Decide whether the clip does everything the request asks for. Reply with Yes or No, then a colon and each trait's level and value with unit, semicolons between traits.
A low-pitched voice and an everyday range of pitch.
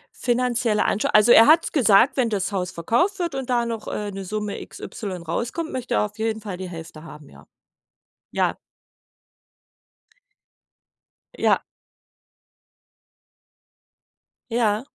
No: high, 220 Hz; average, 3.7 semitones